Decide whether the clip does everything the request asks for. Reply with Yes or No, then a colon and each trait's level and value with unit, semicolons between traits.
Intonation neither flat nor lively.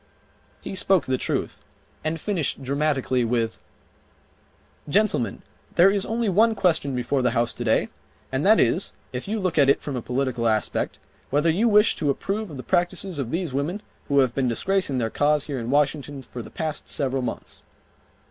No: wide, 6.3 semitones